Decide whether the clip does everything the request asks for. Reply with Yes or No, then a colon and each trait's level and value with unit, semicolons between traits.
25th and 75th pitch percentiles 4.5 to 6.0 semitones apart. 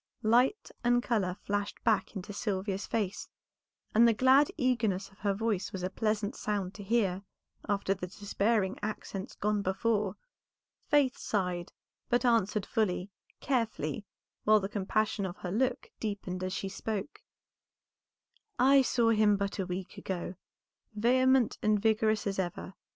No: average, 3.0 semitones